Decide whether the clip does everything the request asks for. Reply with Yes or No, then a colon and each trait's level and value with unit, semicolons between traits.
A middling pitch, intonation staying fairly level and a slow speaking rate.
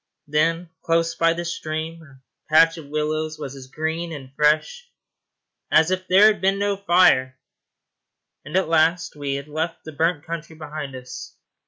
No: medium, 160 Hz; narrow, 2.2 semitones; average, 165 wpm